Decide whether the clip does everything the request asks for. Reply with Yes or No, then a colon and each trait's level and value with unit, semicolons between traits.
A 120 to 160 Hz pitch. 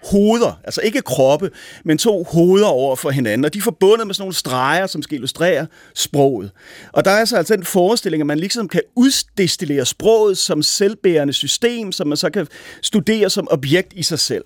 No: medium, 180 Hz